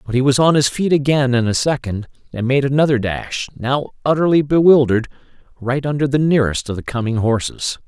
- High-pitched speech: No, low, 130 Hz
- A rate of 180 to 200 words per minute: Yes, average, 190 wpm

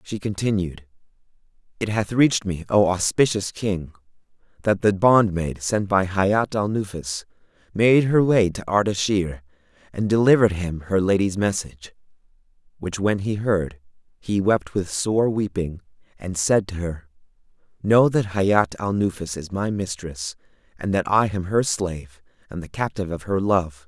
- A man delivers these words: Yes, male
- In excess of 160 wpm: No, average, 155 wpm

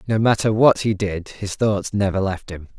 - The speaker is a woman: No, male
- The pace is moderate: No, fast, 215 wpm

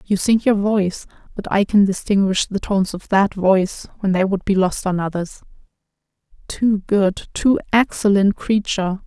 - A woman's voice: Yes, female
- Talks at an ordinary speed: Yes, average, 165 wpm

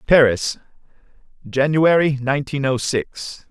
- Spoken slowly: Yes, slow, 85 wpm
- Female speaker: No, male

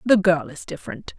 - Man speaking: No, female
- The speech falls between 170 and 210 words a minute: Yes, average, 200 wpm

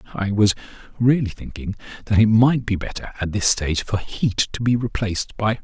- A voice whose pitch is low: Yes, low, 105 Hz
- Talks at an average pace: Yes, average, 190 wpm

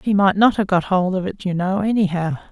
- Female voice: Yes, female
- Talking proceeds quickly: Yes, fast, 260 wpm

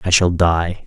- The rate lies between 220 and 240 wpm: No, fast, 210 wpm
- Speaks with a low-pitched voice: Yes, very low, 85 Hz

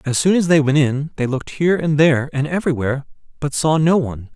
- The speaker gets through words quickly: Yes, fast, 235 wpm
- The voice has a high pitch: No, medium, 145 Hz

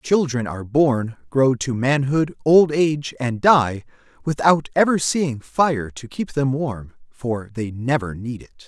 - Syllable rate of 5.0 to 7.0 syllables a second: No, 3.9 syllables/s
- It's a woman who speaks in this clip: No, male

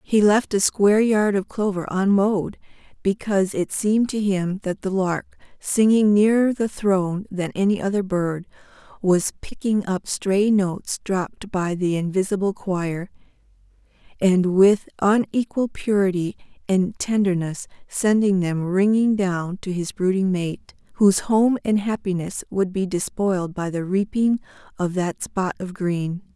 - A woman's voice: Yes, female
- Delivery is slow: No, average, 145 wpm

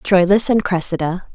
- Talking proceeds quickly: No, slow, 135 wpm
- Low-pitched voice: No, medium, 185 Hz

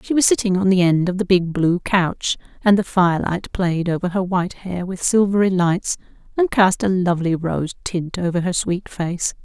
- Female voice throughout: Yes, female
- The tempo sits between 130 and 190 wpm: No, fast, 205 wpm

